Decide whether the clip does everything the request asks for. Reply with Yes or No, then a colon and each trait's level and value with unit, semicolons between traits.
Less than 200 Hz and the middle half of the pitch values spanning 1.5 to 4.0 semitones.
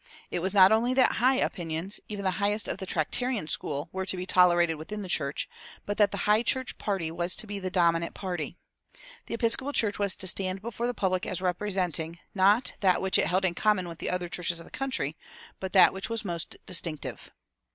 Yes: high, 190 Hz; average, 3.3 semitones